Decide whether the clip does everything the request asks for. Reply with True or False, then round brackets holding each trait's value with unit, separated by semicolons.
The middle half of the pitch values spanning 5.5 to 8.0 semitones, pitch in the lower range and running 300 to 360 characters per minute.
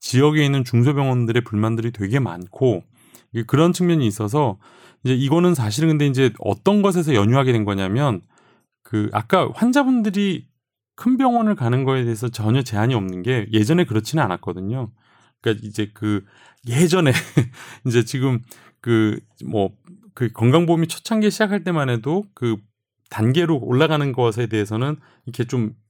True (6.0 semitones; 125 Hz; 330 characters per minute)